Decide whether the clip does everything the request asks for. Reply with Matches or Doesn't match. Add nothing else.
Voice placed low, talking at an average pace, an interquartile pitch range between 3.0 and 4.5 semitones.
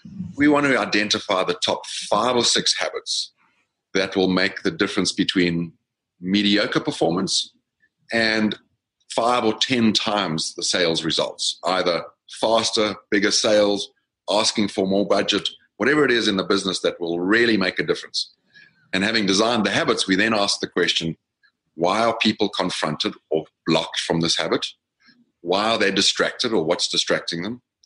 Matches